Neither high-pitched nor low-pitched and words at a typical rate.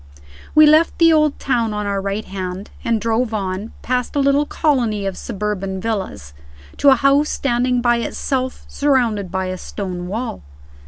No: high, 230 Hz; average, 165 wpm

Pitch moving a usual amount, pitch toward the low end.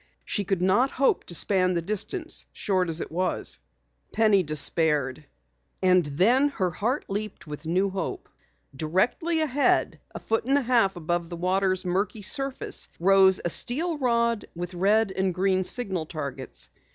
No: average, 4.7 semitones; high, 190 Hz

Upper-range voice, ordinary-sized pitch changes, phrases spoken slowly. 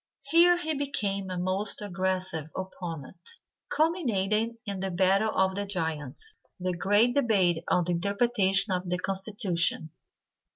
Yes: high, 195 Hz; average, 3.5 semitones; slow, 130 wpm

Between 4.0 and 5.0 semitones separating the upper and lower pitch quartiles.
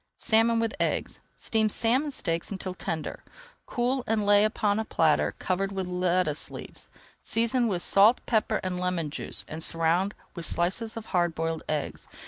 Yes: average, 4.5 semitones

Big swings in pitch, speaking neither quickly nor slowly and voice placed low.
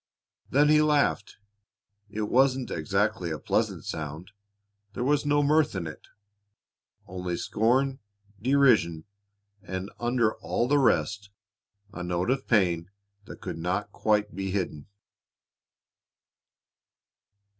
No: wide, 6.8 semitones; slow, 115 wpm; low, 105 Hz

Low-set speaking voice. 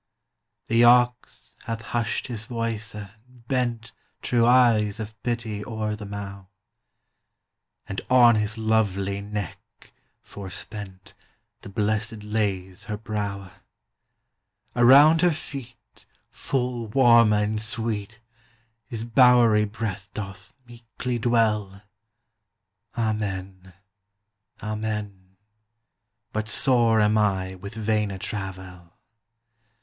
Yes: low, 110 Hz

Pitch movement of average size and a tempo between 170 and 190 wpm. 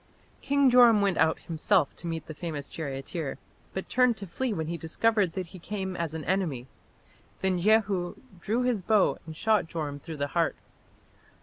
Yes: average, 4.7 semitones; average, 180 wpm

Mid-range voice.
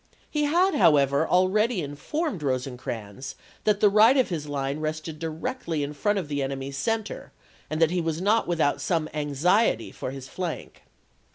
Yes: medium, 160 Hz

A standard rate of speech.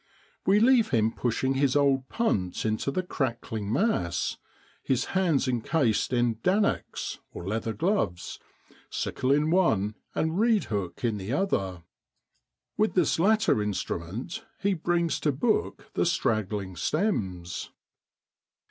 No: slow, 120 wpm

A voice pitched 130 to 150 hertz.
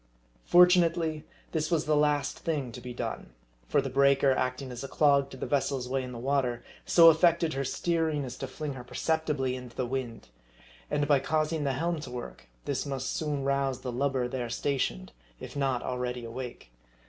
Yes: low, 135 Hz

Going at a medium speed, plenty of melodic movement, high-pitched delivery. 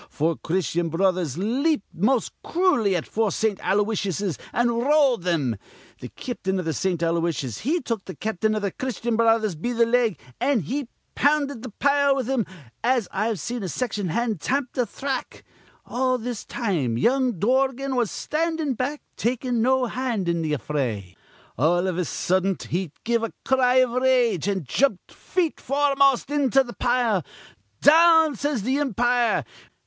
Yes: average, 165 wpm; wide, 5.8 semitones; high, 235 Hz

